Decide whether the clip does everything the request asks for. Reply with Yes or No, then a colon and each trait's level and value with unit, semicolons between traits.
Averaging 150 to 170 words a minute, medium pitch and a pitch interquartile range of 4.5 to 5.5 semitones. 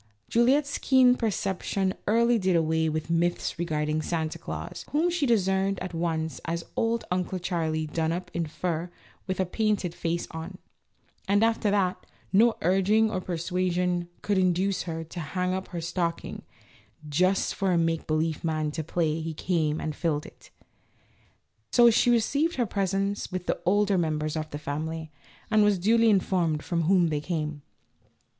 No: average, 165 wpm; medium, 180 Hz; average, 3.7 semitones